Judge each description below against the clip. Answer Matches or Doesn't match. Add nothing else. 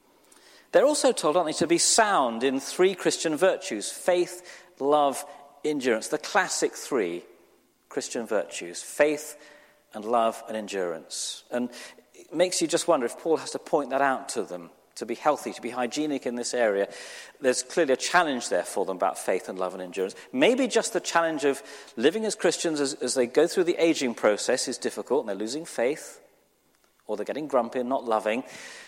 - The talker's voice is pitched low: Doesn't match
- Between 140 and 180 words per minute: Doesn't match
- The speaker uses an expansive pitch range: Matches